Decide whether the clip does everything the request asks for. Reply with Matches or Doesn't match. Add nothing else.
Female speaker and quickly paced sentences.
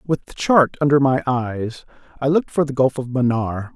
Doesn't match